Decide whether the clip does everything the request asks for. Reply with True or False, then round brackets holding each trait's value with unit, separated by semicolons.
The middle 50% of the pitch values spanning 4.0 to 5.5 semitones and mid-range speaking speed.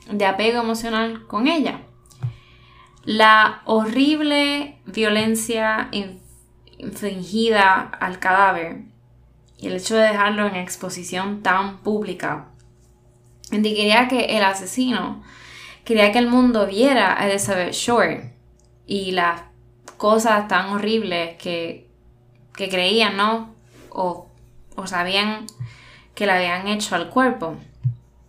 False (4.6 semitones; 105 wpm)